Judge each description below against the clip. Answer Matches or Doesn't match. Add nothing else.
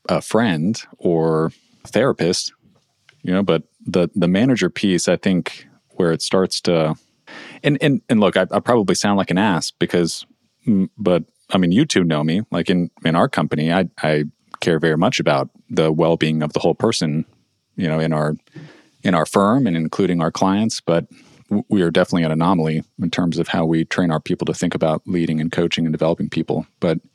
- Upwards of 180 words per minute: Matches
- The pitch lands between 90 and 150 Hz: Doesn't match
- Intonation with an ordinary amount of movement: Doesn't match